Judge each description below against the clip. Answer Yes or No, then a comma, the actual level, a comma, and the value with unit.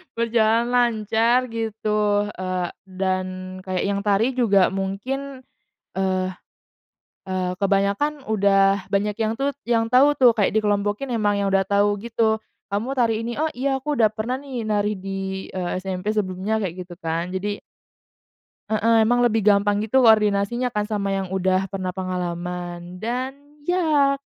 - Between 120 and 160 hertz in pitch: No, high, 210 Hz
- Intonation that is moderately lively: Yes, average, 3.4 semitones